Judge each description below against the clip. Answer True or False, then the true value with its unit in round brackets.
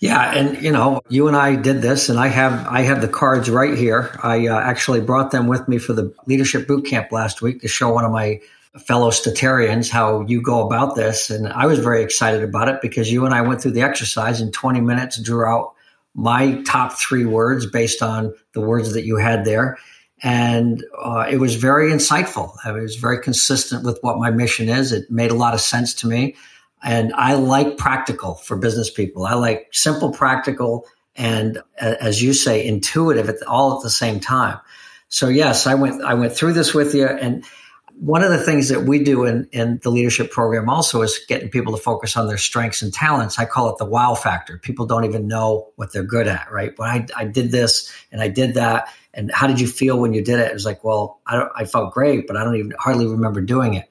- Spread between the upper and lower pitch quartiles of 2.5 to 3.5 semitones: True (2.8 semitones)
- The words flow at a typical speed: False (230 wpm)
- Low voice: True (120 Hz)